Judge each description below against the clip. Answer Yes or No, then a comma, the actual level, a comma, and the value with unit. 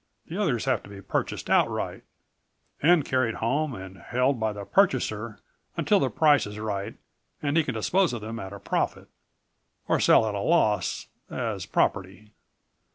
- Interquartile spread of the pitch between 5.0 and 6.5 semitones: Yes, wide, 5.5 semitones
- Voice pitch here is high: No, low, 115 Hz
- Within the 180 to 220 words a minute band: No, average, 165 wpm